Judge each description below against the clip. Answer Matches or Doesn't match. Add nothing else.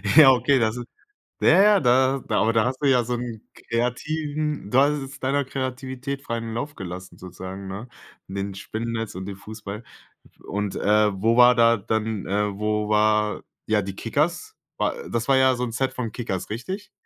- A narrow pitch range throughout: Doesn't match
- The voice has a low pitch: Matches